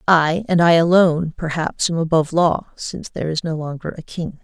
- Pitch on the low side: No, medium, 165 Hz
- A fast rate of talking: No, average, 190 wpm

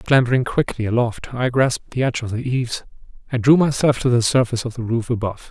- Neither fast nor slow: No, fast, 220 wpm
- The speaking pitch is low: Yes, low, 120 Hz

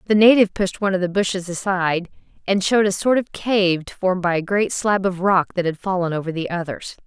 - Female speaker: Yes, female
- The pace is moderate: No, fast, 230 wpm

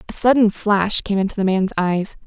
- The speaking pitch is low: No, high, 200 Hz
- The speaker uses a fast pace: Yes, fast, 210 wpm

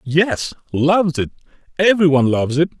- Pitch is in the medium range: Yes, medium, 155 Hz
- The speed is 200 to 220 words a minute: No, average, 150 wpm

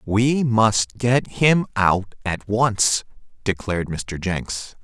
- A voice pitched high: No, low, 105 Hz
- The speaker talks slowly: Yes, slow, 125 wpm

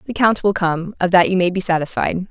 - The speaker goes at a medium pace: No, fast, 260 wpm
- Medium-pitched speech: Yes, medium, 180 Hz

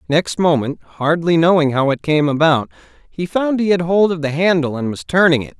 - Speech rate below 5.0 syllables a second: No, 5.3 syllables/s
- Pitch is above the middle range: No, medium, 155 Hz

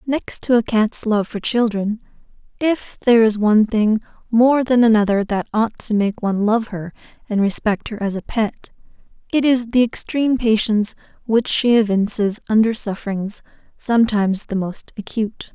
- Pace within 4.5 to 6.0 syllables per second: Yes, 5.0 syllables/s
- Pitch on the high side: Yes, high, 220 Hz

